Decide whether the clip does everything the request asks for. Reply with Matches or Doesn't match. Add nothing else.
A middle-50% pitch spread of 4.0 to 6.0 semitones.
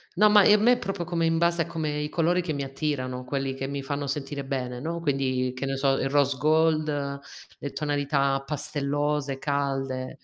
Doesn't match